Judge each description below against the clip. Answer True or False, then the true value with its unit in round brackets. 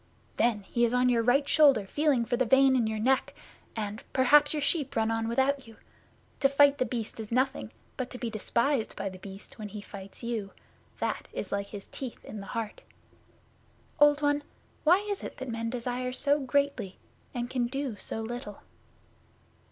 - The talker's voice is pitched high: True (245 Hz)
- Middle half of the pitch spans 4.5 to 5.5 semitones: False (3.8 semitones)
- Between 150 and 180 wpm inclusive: False (190 wpm)